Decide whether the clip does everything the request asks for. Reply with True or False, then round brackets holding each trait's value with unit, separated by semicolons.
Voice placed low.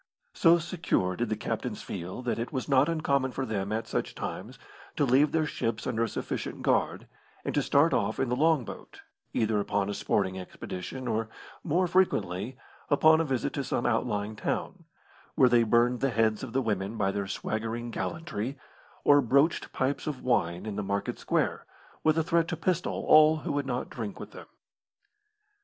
True (125 Hz)